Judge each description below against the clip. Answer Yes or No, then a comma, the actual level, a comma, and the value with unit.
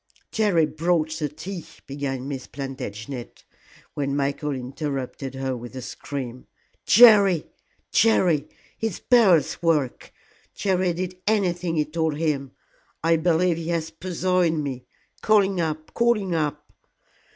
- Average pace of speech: No, slow, 130 wpm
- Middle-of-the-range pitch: Yes, medium, 160 Hz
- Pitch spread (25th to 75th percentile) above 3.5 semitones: Yes, average, 4.6 semitones